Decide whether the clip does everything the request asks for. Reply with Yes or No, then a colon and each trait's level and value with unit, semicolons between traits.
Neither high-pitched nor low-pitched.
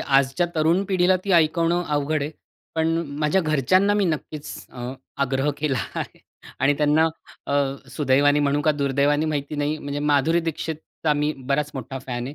Yes: medium, 150 Hz